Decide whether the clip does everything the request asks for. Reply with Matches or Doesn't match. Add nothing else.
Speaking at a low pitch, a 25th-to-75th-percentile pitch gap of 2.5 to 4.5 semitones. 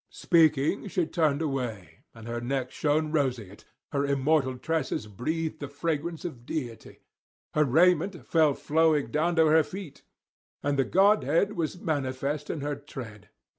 Doesn't match